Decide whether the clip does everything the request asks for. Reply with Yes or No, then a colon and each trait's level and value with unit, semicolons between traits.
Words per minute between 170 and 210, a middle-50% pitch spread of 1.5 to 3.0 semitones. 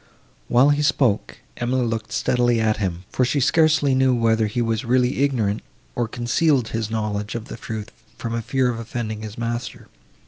Yes: average, 180 wpm; average, 2.7 semitones